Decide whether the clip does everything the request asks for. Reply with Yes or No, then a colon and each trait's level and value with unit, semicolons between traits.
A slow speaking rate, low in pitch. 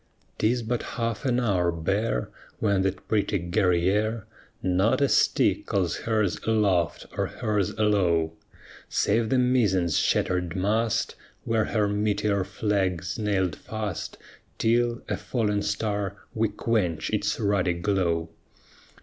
Yes: slow, 125 wpm; low, 105 Hz